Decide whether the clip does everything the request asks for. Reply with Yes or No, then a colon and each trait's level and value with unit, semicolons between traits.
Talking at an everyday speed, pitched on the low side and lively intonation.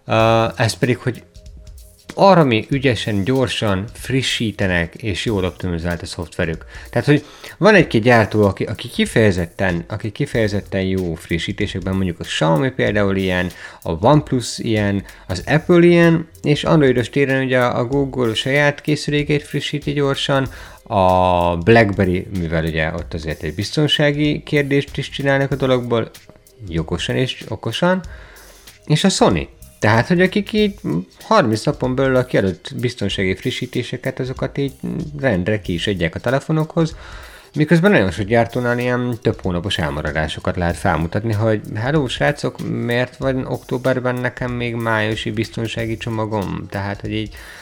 Yes: average, 140 wpm; low, 115 Hz; wide, 6.2 semitones